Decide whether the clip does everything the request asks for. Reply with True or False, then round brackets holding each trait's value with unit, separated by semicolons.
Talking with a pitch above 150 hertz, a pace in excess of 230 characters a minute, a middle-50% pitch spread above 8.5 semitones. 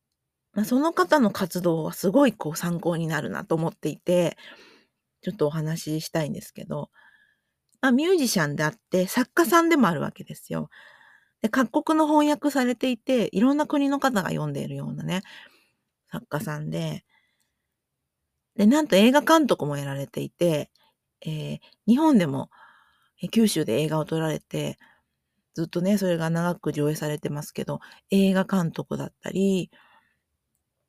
True (185 Hz; 300 characters per minute; 9.0 semitones)